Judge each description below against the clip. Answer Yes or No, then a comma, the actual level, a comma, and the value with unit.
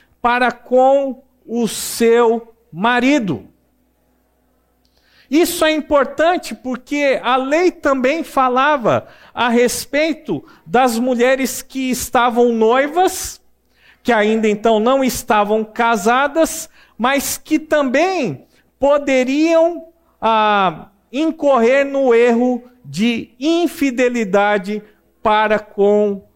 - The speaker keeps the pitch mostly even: No, average, 3.7 semitones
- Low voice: No, very high, 255 Hz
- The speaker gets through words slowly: Yes, slow, 85 wpm